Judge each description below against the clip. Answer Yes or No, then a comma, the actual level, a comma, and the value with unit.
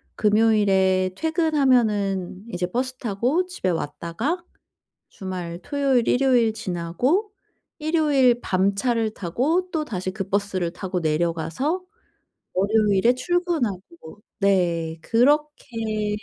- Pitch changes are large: Yes, wide, 6.5 semitones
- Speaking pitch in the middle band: No, high, 215 Hz